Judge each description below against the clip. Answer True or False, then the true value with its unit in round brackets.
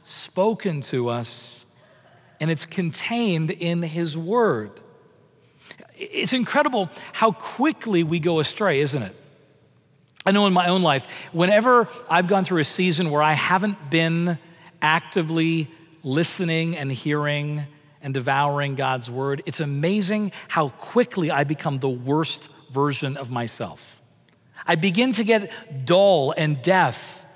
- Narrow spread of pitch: False (4.6 semitones)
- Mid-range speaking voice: True (165 Hz)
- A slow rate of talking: True (130 wpm)